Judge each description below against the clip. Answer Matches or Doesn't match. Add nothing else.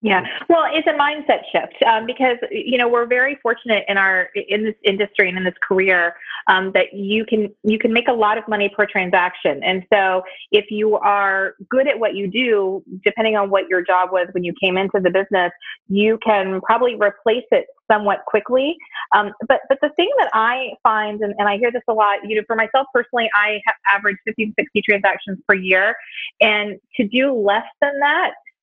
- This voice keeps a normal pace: Doesn't match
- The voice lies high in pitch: Matches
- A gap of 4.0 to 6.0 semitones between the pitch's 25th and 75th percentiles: Doesn't match